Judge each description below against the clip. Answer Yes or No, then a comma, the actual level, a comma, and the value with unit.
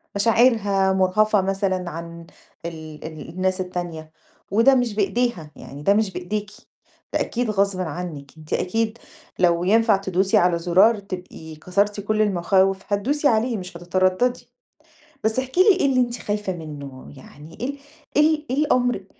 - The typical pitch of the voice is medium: No, high, 195 Hz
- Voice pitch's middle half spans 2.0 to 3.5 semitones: No, average, 4.1 semitones